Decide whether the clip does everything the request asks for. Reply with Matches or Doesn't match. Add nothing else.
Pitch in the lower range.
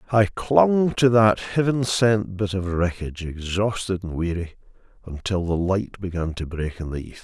Matches